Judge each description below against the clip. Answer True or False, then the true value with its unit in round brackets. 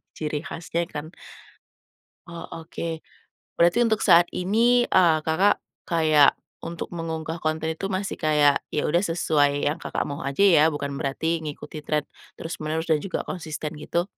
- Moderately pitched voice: True (160 Hz)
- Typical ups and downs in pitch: False (2.3 semitones)